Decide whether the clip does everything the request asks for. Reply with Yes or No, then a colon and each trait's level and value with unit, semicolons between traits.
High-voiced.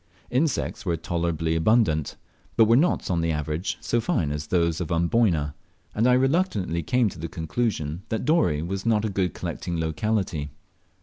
No: very low, 85 Hz